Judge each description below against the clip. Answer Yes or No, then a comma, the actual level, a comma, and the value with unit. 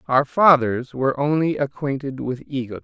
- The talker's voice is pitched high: No, low, 135 Hz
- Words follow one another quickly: No, average, 150 wpm